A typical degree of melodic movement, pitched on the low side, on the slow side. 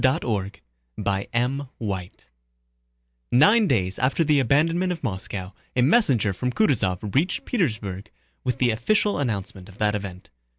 No: wide, 6.6 semitones; low, 120 Hz; slow, 125 wpm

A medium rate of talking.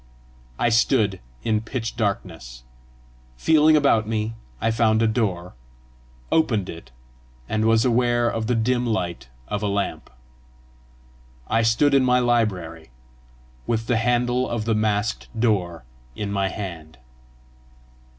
No: slow, 130 wpm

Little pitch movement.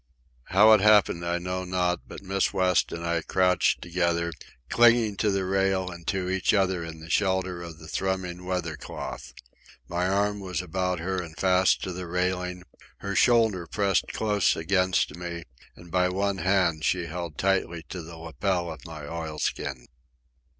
Yes: narrow, 2.0 semitones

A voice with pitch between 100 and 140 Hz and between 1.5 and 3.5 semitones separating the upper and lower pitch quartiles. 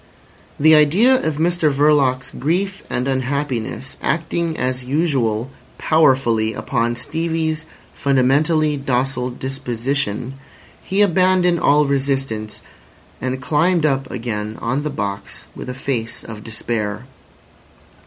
No: low, 135 Hz; average, 4.2 semitones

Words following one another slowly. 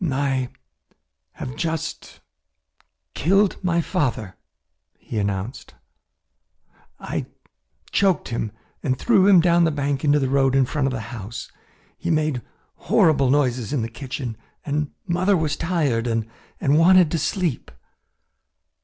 Yes: slow, 125 wpm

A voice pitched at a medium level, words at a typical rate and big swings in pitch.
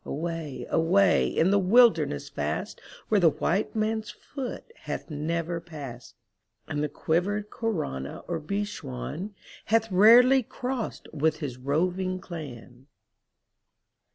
No: medium, 175 Hz; slow, 125 wpm; wide, 5.8 semitones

